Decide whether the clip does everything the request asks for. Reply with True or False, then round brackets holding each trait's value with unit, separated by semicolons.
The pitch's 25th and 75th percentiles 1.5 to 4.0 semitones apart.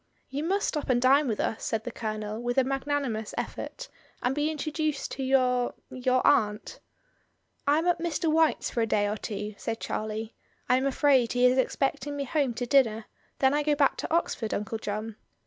False (4.5 semitones)